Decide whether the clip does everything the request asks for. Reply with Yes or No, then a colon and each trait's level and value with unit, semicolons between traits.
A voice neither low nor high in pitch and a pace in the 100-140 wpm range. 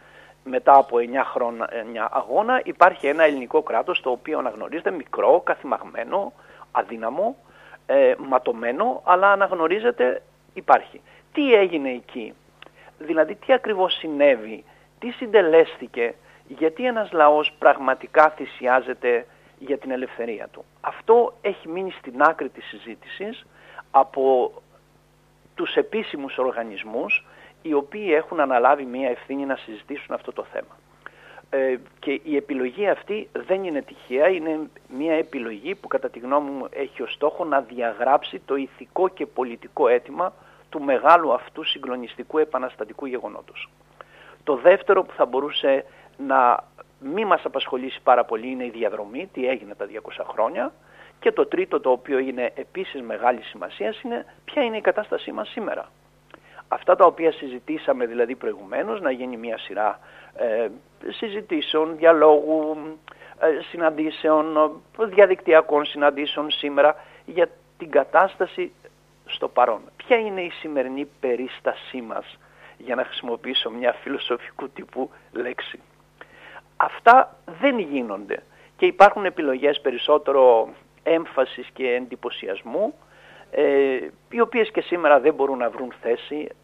Yes: medium, 155 Hz; average, 125 wpm